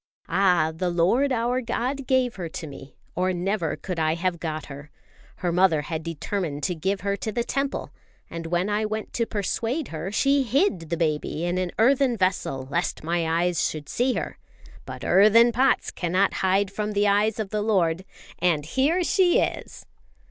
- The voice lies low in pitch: No, high, 190 Hz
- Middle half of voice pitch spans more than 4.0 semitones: Yes, wide, 5.6 semitones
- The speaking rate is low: No, average, 185 wpm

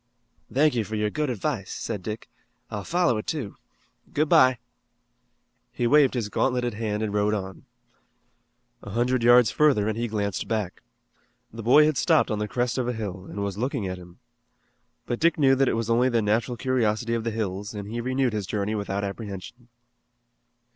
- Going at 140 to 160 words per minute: No, average, 190 wpm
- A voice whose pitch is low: Yes, low, 115 Hz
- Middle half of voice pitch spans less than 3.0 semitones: No, average, 3.5 semitones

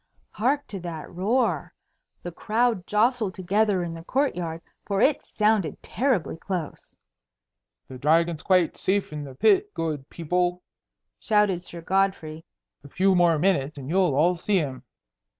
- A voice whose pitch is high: No, medium, 180 Hz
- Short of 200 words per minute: Yes, average, 150 wpm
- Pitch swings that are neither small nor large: Yes, average, 4.2 semitones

